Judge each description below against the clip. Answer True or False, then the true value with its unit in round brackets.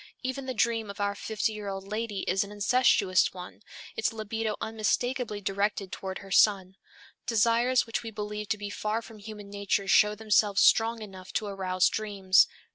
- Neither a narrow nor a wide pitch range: False (2.1 semitones)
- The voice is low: False (210 Hz)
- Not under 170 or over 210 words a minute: True (175 wpm)